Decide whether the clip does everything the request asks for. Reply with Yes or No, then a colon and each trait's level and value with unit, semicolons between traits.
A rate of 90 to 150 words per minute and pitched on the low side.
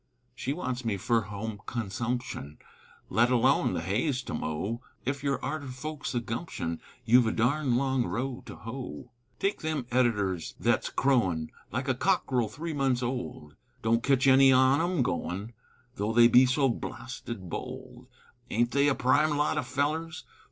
No: average, 160 wpm; low, 125 Hz